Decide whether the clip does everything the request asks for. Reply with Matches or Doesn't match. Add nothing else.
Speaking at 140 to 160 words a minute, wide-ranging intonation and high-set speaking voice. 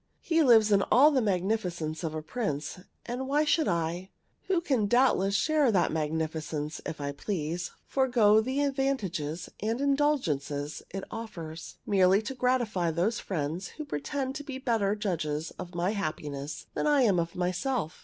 Matches